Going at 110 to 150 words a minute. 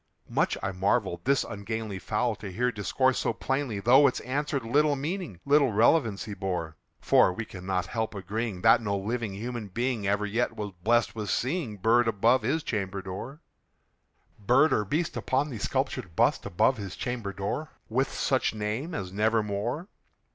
No: average, 165 wpm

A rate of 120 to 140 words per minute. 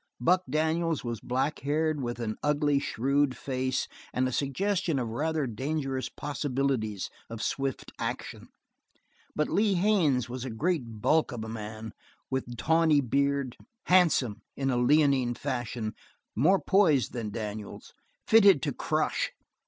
Yes: slow, 135 wpm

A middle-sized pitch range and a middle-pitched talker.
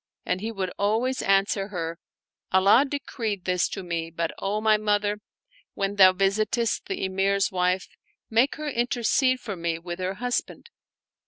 No: average, 3.4 semitones; high, 200 Hz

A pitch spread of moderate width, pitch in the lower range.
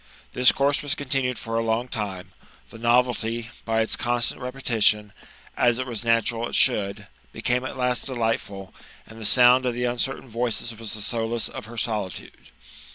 No: narrow, 1.9 semitones; low, 115 Hz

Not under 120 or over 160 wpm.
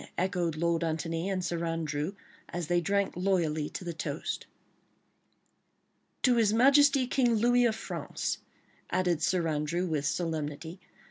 Yes: slow, 135 wpm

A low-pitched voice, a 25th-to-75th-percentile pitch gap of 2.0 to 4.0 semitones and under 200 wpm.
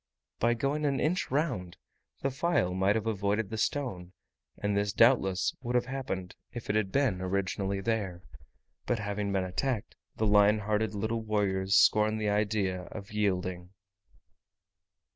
Yes: low, 105 Hz; average, 3.1 semitones; average, 150 wpm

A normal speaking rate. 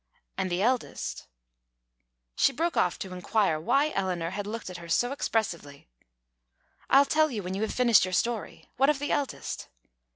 Yes: average, 175 wpm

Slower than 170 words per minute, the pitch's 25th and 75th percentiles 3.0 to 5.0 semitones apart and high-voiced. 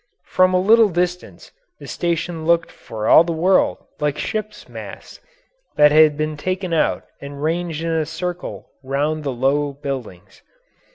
No: average, 155 wpm; average, 3.4 semitones; medium, 160 Hz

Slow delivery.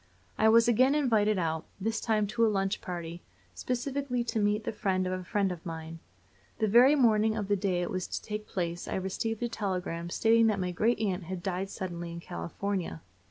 No: fast, 205 wpm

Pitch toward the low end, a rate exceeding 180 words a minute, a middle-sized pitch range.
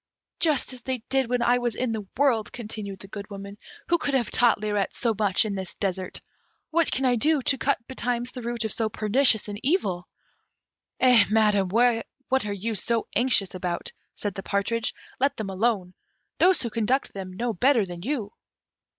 No: high, 225 Hz; average, 190 wpm; average, 3.9 semitones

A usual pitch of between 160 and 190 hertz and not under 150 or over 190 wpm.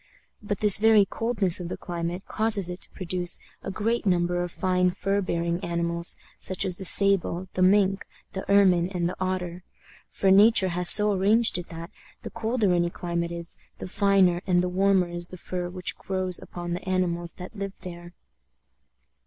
Yes: medium, 185 Hz; average, 180 wpm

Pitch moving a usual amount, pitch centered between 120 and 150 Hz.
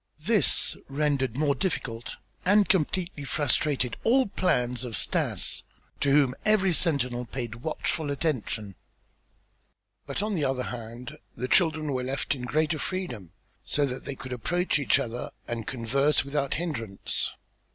Yes: average, 4.3 semitones; medium, 140 Hz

